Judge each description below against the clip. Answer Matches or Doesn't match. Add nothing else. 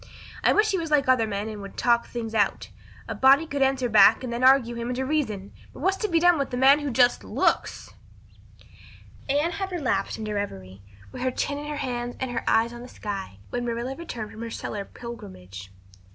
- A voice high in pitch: Matches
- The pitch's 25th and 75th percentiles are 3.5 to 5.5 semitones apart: Matches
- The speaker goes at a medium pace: Doesn't match